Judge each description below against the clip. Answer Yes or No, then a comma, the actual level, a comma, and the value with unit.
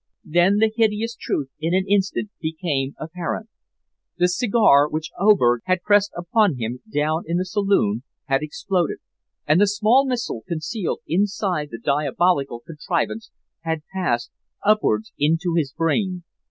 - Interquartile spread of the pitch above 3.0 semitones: Yes, average, 5.3 semitones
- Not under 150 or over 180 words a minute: No, average, 140 wpm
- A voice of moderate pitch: Yes, medium, 175 Hz